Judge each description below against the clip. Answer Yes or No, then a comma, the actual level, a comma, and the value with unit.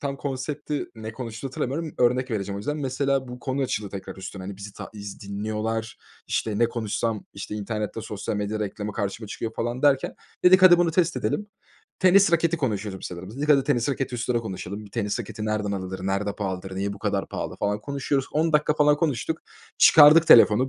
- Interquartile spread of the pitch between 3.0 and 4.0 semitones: No, wide, 5.4 semitones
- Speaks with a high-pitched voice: No, low, 115 Hz